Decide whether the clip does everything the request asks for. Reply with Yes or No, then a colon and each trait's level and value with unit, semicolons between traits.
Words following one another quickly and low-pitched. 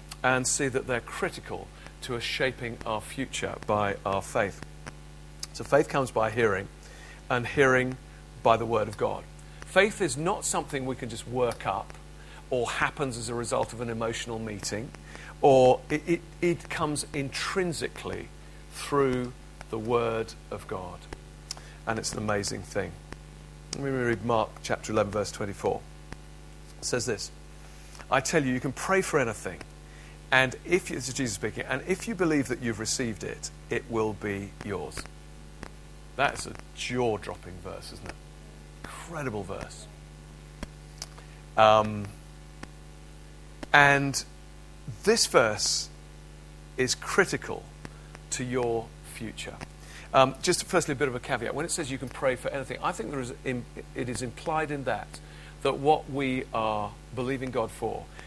No: average, 150 wpm; low, 105 Hz